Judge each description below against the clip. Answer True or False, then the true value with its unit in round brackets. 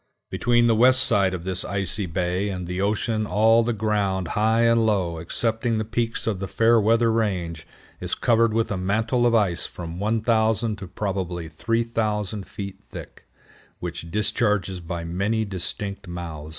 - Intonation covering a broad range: False (3.6 semitones)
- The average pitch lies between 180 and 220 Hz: False (105 Hz)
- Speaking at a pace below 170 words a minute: True (160 wpm)